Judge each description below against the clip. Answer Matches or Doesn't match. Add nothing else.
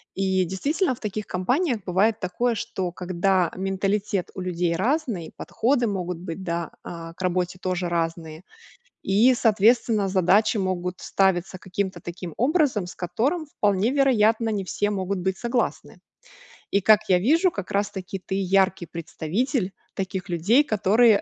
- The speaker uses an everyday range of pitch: Matches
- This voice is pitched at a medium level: Doesn't match